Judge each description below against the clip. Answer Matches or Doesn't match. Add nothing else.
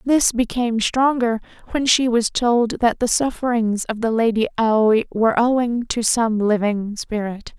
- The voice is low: Doesn't match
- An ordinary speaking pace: Matches